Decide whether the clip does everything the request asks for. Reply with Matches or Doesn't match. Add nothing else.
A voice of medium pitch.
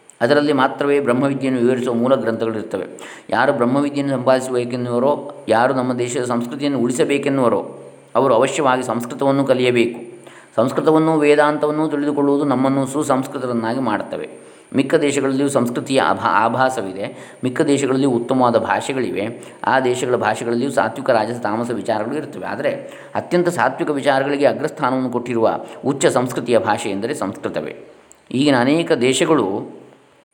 Doesn't match